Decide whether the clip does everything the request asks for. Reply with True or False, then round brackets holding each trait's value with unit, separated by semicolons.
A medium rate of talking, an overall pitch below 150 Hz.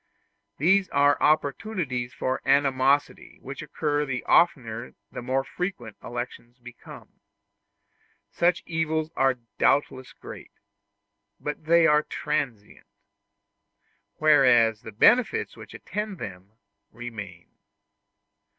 False (95 wpm; 135 Hz)